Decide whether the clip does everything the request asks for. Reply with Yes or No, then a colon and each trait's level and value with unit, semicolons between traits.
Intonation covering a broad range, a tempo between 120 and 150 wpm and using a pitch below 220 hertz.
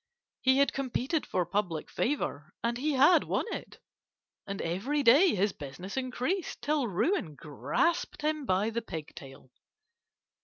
No: wide, 8.4 semitones; average, 140 wpm; high, 235 Hz